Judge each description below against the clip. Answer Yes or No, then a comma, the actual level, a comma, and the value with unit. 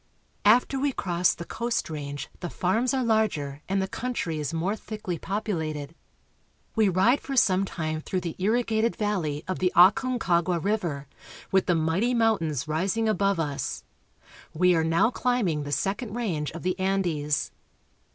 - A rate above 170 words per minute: No, average, 160 wpm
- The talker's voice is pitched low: No, medium, 185 Hz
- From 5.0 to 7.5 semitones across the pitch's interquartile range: Yes, wide, 5.4 semitones